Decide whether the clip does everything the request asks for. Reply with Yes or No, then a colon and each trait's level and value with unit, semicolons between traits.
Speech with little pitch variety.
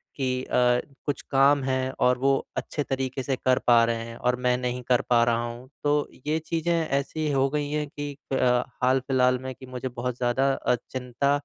Yes: narrow, 2.0 semitones